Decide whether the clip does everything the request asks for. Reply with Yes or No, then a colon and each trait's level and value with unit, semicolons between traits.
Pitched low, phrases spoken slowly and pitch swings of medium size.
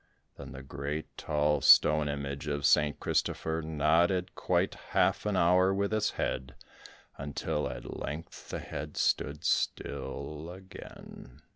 Yes: very low, 75 Hz; slow, 130 wpm; average, 3.2 semitones